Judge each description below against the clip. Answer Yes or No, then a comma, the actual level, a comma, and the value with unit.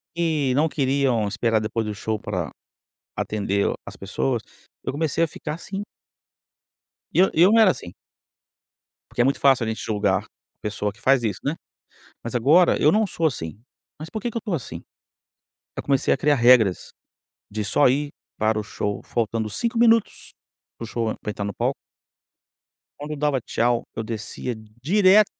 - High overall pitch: No, low, 125 Hz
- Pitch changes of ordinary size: No, wide, 6.6 semitones